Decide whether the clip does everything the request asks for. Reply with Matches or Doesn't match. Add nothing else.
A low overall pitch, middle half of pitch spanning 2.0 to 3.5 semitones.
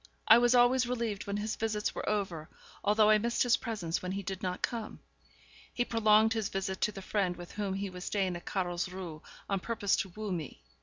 Doesn't match